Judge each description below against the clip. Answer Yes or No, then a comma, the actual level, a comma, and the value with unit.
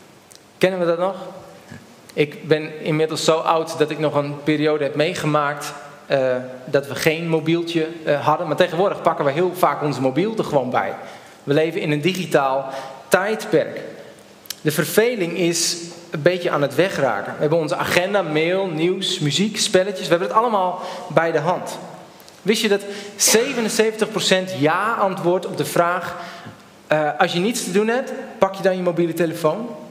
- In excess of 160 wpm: Yes, average, 170 wpm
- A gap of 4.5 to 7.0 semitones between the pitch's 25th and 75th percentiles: No, average, 3.5 semitones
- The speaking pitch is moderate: Yes, medium, 170 Hz